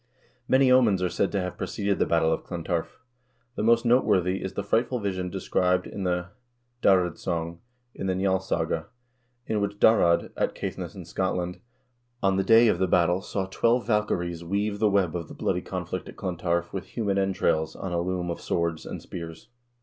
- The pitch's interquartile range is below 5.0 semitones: Yes, average, 2.8 semitones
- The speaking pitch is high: No, very low, 95 Hz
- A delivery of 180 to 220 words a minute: Yes, average, 190 wpm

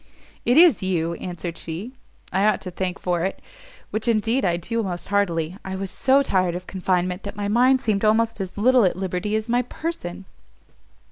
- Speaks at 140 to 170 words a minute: No, average, 190 wpm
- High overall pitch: Yes, high, 195 Hz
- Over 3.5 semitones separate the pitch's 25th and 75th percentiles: Yes, average, 4.1 semitones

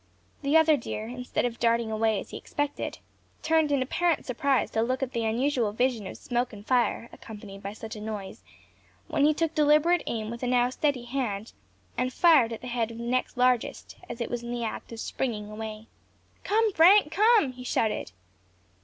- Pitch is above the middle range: Yes, high, 245 Hz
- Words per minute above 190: Yes, average, 200 wpm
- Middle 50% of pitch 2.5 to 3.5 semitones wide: No, average, 4.4 semitones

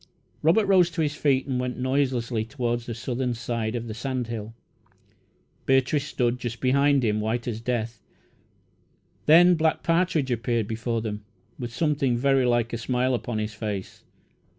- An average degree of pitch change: Yes, average, 3.1 semitones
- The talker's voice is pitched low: Yes, low, 125 Hz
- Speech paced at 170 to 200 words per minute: No, average, 160 wpm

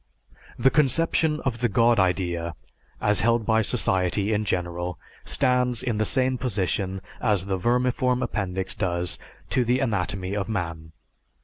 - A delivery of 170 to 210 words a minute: No, average, 140 wpm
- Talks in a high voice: No, low, 105 Hz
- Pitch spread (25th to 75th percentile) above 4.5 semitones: Yes, average, 5.0 semitones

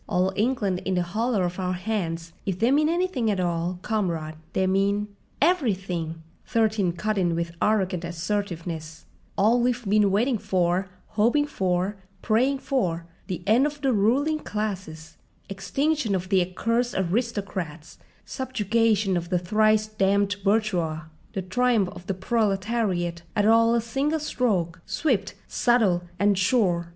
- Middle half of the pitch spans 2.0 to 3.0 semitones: No, average, 4.3 semitones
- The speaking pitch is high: Yes, high, 200 Hz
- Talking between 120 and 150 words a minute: Yes, average, 140 wpm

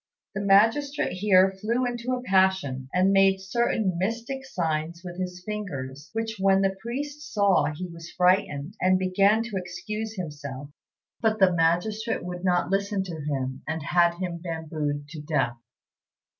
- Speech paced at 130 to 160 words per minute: Yes, average, 155 wpm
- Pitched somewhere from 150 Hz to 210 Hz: Yes, medium, 185 Hz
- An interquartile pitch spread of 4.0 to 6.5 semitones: Yes, average, 4.4 semitones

